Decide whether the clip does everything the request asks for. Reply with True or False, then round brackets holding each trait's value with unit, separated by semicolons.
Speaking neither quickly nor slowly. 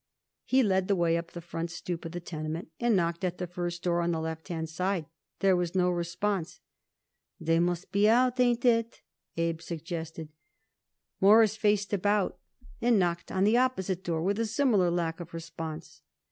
True (180 wpm)